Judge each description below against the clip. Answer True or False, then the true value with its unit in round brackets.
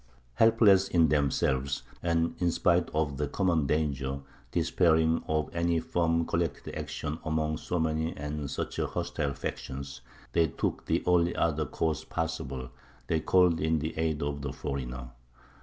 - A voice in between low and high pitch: False (80 Hz)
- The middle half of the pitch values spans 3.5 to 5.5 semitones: False (2.7 semitones)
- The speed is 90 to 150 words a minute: True (145 wpm)